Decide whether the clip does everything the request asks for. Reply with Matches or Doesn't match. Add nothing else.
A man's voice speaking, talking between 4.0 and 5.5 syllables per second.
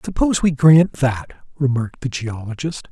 Matches